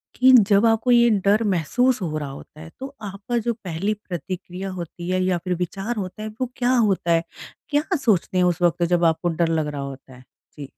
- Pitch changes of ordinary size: Yes, average, 4.7 semitones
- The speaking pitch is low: No, medium, 185 Hz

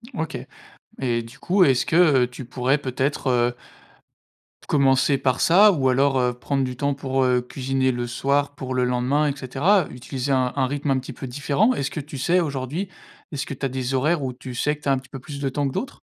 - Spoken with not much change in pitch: Yes, narrow, 2.0 semitones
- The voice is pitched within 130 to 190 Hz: Yes, low, 135 Hz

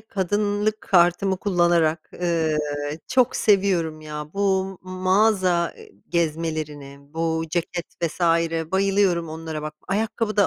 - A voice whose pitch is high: No, medium, 175 Hz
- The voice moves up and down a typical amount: Yes, average, 3.5 semitones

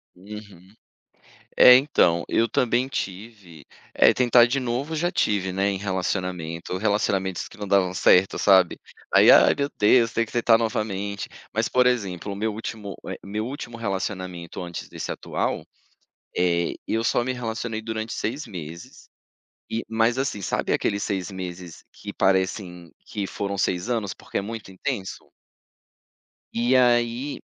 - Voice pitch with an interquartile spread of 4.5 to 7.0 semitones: No, average, 3.8 semitones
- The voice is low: Yes, low, 105 Hz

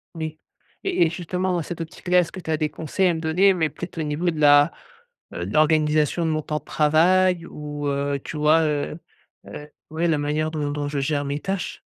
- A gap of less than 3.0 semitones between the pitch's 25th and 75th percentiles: Yes, narrow, 2.4 semitones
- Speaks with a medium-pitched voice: Yes, medium, 155 Hz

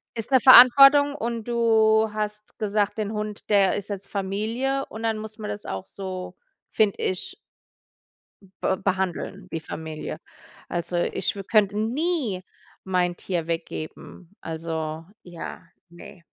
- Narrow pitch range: No, average, 3.7 semitones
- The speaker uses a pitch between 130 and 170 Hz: No, high, 205 Hz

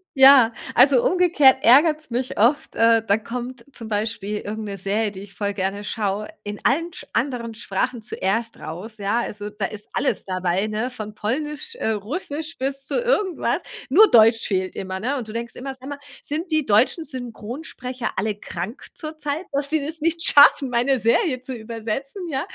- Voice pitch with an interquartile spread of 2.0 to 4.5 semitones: No, average, 5.1 semitones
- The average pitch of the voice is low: No, high, 240 Hz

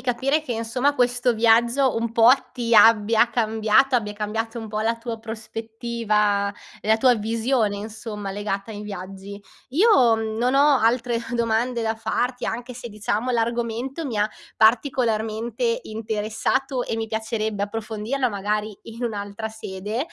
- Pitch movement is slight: Yes, narrow, 2.2 semitones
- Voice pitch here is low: No, high, 225 Hz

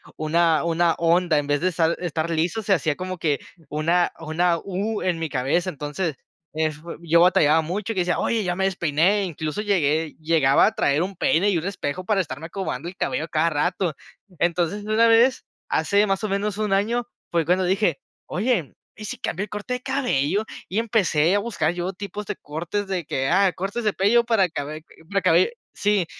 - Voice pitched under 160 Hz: No, medium, 180 Hz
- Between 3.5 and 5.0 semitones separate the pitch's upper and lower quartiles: Yes, average, 4.1 semitones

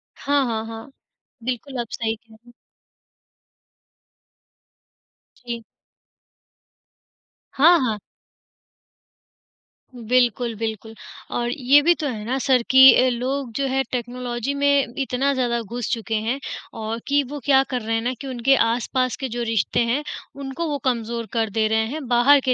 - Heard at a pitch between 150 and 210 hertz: No, high, 245 Hz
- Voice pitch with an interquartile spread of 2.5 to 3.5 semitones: Yes, average, 2.9 semitones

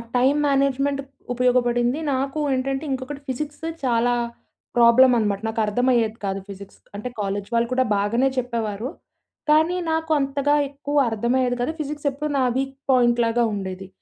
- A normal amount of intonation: Yes, average, 3.1 semitones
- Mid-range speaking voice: No, very high, 250 Hz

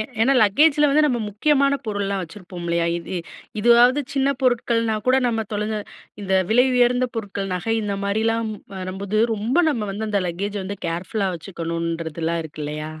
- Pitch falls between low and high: No, high, 205 Hz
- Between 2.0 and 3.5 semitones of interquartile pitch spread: No, average, 4.7 semitones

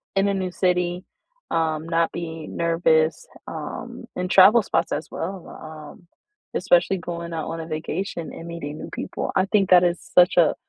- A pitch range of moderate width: No, narrow, 2.2 semitones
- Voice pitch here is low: No, medium, 170 Hz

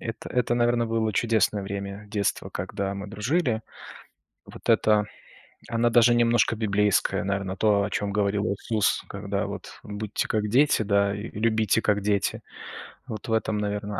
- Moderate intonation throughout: No, narrow, 2.0 semitones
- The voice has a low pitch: Yes, low, 105 Hz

